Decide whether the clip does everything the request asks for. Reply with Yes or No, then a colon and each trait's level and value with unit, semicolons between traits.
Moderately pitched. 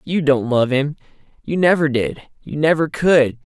Yes: medium, 145 Hz